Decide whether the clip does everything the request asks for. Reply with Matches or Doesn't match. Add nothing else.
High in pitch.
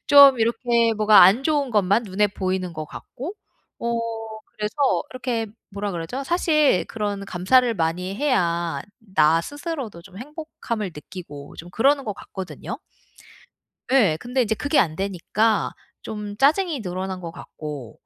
Matches